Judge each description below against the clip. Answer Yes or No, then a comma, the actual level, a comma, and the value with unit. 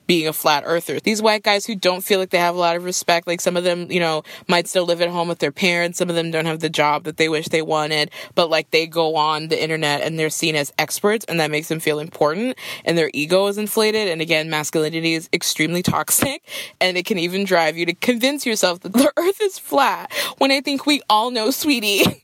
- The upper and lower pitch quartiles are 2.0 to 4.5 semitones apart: No, average, 4.9 semitones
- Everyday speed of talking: No, fast, 250 wpm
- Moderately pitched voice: Yes, medium, 175 Hz